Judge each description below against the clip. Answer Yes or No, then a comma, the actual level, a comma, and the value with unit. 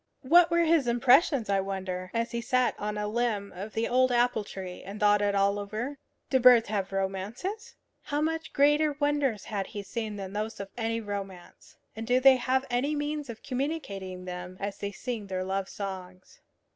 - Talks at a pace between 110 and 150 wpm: No, average, 190 wpm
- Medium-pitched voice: No, high, 225 Hz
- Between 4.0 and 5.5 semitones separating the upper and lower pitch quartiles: Yes, average, 4.9 semitones